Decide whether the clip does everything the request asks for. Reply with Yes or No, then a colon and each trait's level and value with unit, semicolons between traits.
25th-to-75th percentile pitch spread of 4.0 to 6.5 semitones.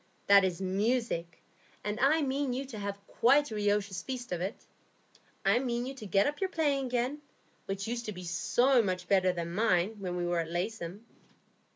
Yes: wide, 5.4 semitones